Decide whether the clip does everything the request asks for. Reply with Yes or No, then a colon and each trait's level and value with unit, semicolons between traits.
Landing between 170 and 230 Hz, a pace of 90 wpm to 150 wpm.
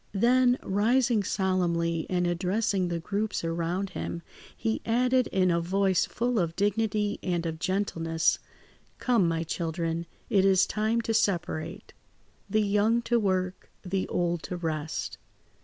Yes: high, 190 Hz; average, 140 wpm